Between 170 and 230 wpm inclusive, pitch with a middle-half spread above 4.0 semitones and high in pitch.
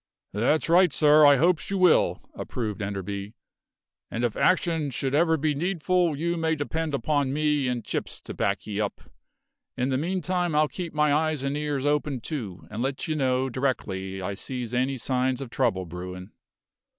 No: average, 175 wpm; average, 4.7 semitones; medium, 140 Hz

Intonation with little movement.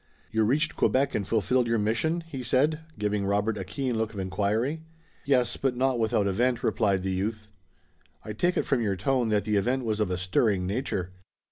No: average, 4.2 semitones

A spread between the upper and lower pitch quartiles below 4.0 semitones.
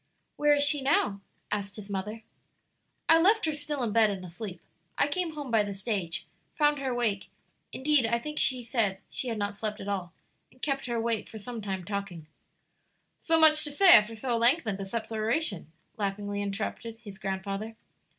No: wide, 5.5 semitones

